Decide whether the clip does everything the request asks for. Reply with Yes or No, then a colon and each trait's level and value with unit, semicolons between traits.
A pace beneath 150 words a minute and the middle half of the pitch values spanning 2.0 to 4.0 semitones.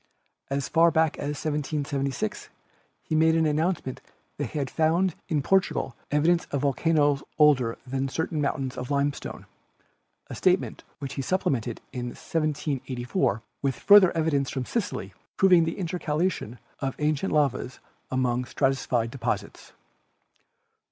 Yes: average, 140 wpm; average, 3.5 semitones